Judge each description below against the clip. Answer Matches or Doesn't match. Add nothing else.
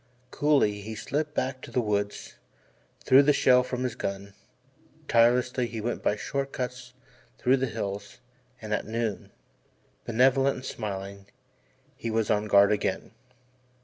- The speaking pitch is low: Matches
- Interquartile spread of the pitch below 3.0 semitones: Doesn't match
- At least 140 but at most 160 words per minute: Matches